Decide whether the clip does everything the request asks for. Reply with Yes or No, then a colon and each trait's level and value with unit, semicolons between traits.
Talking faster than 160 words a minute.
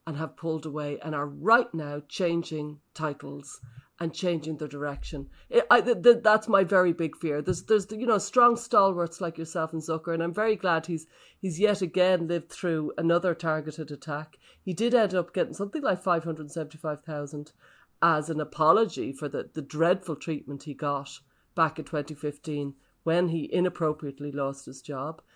Yes: average, 180 wpm